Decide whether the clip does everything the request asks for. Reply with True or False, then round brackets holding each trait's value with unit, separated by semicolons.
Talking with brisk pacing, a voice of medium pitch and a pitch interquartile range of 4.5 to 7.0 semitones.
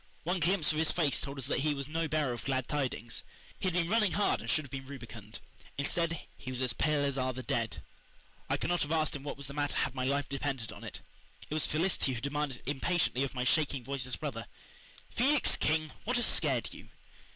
False (230 wpm; 145 Hz; 3.4 semitones)